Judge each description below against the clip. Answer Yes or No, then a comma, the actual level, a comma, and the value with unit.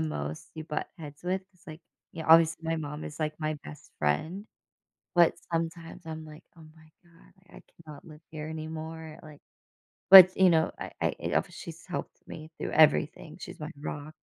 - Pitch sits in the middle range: Yes, medium, 160 Hz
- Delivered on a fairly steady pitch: Yes, narrow, 1.3 semitones